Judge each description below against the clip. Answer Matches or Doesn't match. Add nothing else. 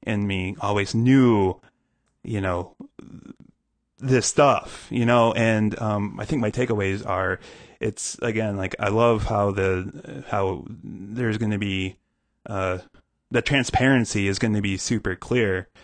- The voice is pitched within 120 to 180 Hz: Doesn't match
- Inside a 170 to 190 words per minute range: Doesn't match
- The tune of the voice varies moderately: Matches